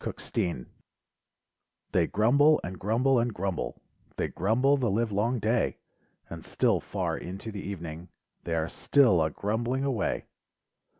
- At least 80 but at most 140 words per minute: Yes, slow, 135 wpm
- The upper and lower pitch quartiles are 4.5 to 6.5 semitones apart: Yes, average, 5.1 semitones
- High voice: No, low, 110 Hz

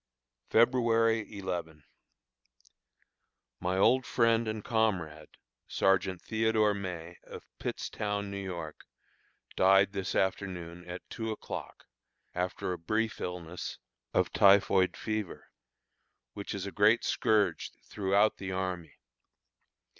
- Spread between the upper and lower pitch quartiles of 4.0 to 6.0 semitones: No, average, 3.3 semitones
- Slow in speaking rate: Yes, slow, 105 wpm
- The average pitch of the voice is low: Yes, low, 100 Hz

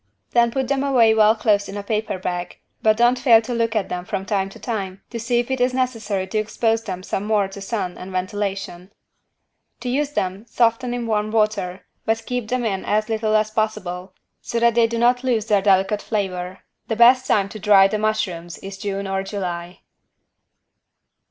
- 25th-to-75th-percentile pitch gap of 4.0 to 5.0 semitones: No, average, 3.3 semitones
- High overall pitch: Yes, high, 215 Hz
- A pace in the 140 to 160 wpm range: No, average, 200 wpm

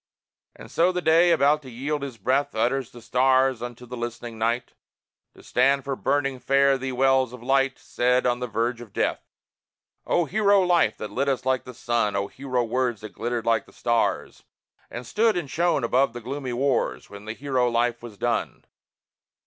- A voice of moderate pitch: No, low, 125 Hz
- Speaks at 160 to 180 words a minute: No, average, 190 wpm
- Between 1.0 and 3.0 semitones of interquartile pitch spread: Yes, narrow, 2.6 semitones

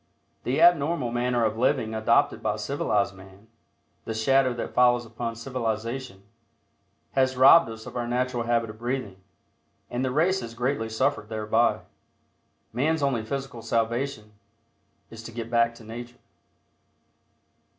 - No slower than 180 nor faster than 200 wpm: No, average, 140 wpm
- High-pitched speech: No, low, 120 Hz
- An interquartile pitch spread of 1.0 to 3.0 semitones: Yes, narrow, 2.6 semitones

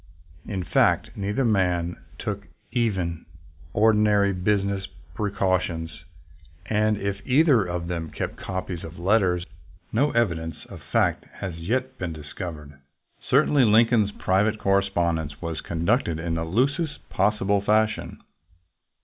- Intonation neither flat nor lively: Yes, average, 4.1 semitones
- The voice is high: No, low, 100 Hz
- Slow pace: Yes, slow, 120 wpm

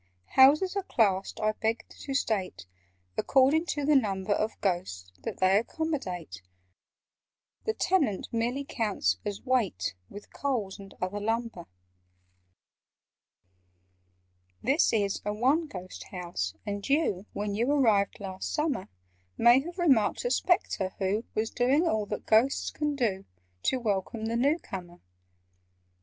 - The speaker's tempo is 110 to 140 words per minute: Yes, slow, 135 wpm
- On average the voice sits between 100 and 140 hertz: No, high, 220 Hz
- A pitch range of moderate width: No, wide, 6.1 semitones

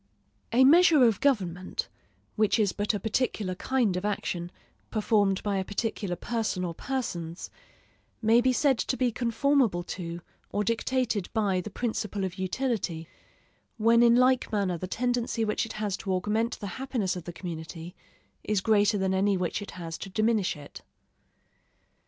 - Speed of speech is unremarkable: Yes, average, 160 wpm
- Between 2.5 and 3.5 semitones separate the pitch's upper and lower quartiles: No, average, 4.3 semitones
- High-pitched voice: Yes, high, 210 Hz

